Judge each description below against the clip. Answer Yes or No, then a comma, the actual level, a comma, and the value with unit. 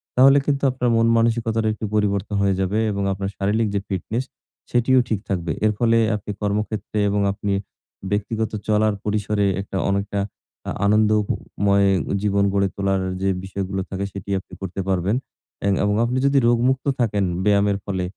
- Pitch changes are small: Yes, narrow, 2.2 semitones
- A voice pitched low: Yes, low, 105 Hz